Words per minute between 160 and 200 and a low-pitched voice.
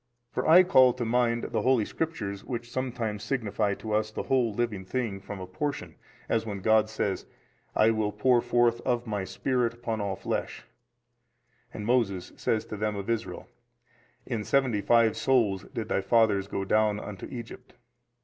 Yes: average, 180 wpm; low, 110 Hz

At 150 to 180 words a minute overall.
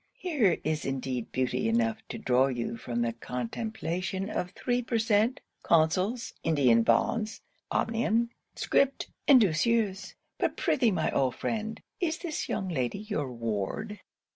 No: average, 140 wpm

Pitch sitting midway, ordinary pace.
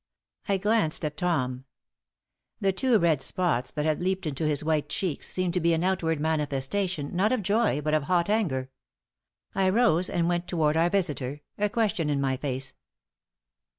Yes: medium, 165 Hz; average, 175 wpm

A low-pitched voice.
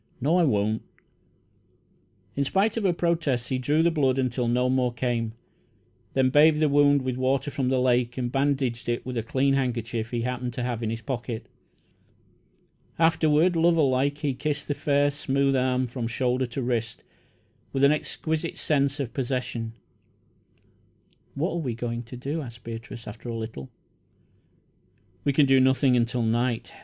Yes: low, 130 Hz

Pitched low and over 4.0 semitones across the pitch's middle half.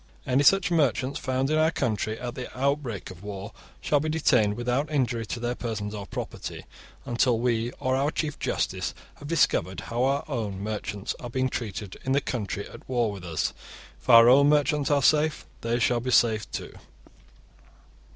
Yes: low, 125 Hz; average, 4.4 semitones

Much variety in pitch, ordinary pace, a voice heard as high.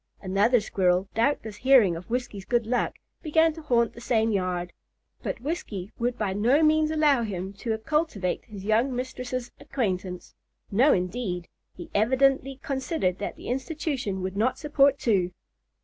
Yes: wide, 5.8 semitones; average, 150 wpm; high, 235 Hz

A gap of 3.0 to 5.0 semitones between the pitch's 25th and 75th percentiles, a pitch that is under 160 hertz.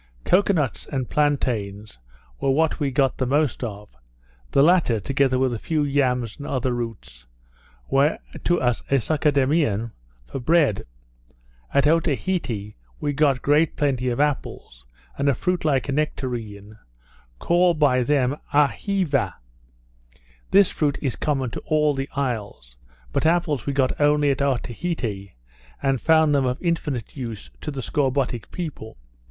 Yes: average, 3.7 semitones; medium, 140 Hz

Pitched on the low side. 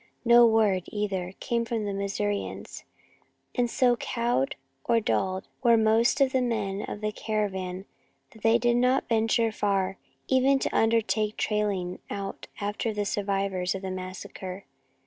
No: high, 210 Hz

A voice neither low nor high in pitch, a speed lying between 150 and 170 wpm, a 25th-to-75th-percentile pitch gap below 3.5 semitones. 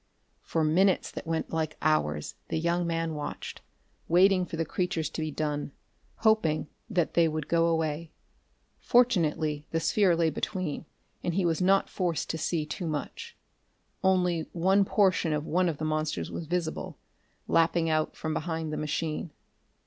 Yes: medium, 165 Hz; average, 160 wpm; narrow, 2.4 semitones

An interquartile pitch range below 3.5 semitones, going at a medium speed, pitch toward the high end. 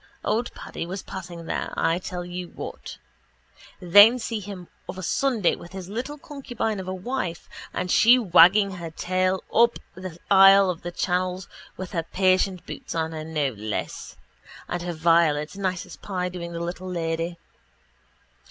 No: narrow, 2.5 semitones; average, 170 wpm; medium, 180 Hz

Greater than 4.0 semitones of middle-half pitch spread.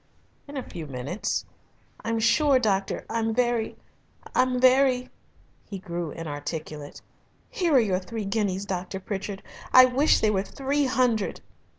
Yes: wide, 5.4 semitones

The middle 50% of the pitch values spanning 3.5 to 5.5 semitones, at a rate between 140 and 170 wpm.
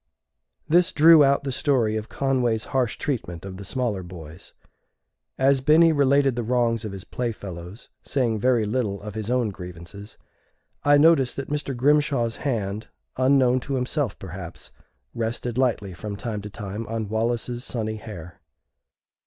Yes: average, 4.6 semitones; average, 150 wpm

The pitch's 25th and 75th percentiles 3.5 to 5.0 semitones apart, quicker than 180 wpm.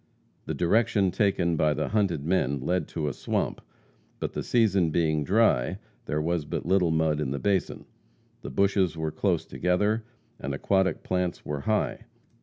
No: average, 4.3 semitones; average, 165 wpm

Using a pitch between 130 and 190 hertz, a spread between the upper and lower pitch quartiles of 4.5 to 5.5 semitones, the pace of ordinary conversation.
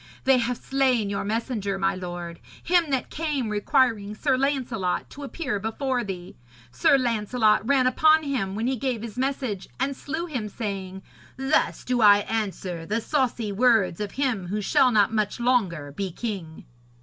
No: high, 225 Hz; average, 4.8 semitones; average, 165 wpm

